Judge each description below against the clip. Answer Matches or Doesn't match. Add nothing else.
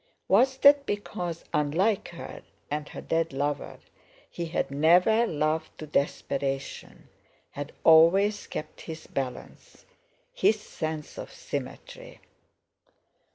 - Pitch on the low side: Doesn't match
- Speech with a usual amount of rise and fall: Doesn't match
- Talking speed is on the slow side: Matches